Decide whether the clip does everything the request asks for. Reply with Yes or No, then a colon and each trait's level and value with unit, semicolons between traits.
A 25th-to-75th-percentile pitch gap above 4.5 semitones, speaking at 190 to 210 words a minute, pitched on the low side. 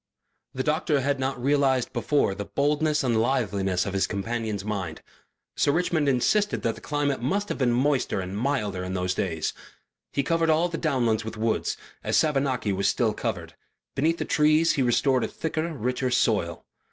No: wide, 5.6 semitones; average, 175 wpm; low, 130 Hz